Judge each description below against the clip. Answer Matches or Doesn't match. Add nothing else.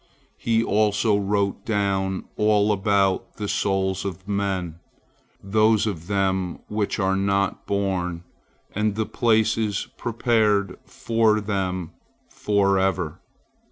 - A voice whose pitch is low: Matches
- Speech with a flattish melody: Matches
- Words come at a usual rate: Doesn't match